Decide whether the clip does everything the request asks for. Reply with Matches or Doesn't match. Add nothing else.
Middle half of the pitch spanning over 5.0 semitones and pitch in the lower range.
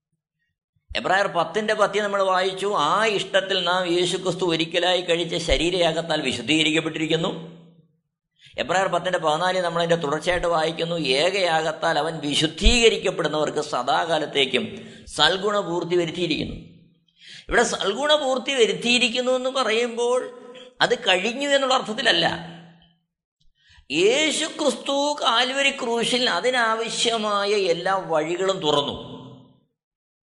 Doesn't match